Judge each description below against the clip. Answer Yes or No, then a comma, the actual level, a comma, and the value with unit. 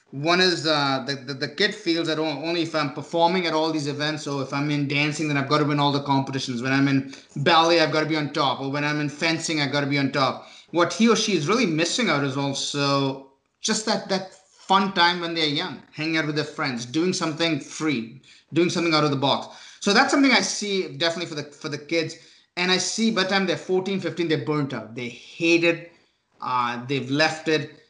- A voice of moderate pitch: Yes, medium, 155 Hz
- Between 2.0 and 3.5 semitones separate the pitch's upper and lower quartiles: Yes, average, 3.2 semitones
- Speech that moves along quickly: Yes, fast, 235 wpm